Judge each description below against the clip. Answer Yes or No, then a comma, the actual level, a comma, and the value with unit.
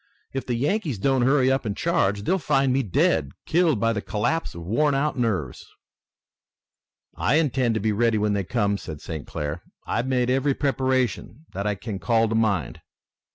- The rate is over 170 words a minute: Yes, average, 185 wpm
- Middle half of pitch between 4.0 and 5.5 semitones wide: Yes, average, 5.0 semitones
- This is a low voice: Yes, low, 115 Hz